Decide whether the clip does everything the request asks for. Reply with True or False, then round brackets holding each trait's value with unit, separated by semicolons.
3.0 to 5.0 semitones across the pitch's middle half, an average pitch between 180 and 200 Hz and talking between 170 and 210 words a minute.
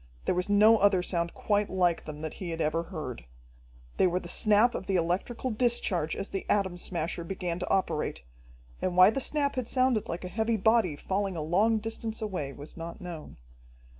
True (4.3 semitones; 185 Hz; 195 wpm)